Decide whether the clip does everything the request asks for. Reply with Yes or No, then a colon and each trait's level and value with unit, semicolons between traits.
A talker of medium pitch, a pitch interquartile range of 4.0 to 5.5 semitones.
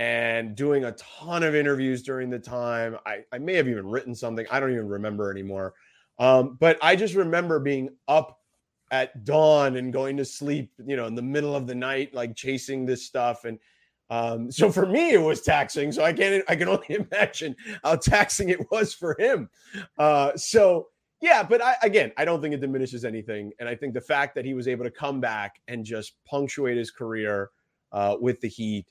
No: low, 130 Hz; average, 4.6 semitones